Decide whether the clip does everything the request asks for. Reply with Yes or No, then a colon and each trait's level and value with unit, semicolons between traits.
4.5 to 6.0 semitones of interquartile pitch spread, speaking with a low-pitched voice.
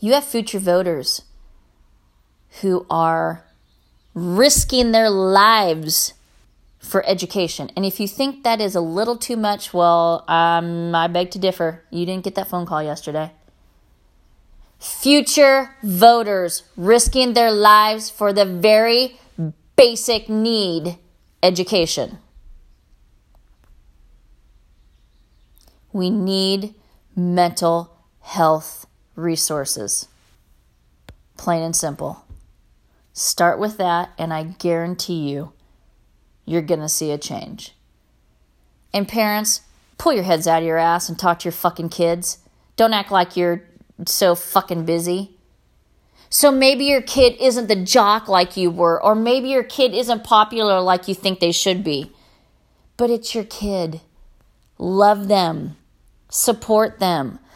No: average, 4.9 semitones; medium, 180 Hz